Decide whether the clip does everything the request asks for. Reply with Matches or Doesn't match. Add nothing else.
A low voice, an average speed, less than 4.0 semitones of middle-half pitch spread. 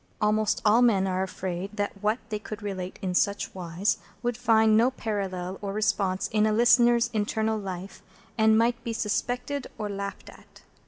Doesn't match